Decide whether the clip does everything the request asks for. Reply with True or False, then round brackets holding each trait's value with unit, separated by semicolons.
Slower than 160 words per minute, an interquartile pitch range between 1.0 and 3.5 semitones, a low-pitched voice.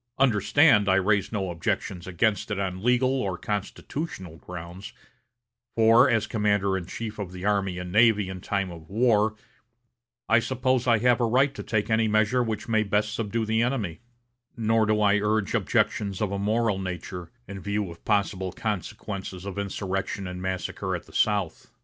False (175 wpm; 2.9 semitones; 105 Hz)